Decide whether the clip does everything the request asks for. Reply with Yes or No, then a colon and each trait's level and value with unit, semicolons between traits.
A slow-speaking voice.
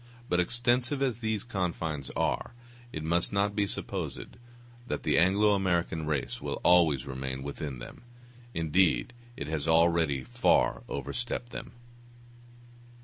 Yes: slow, 130 wpm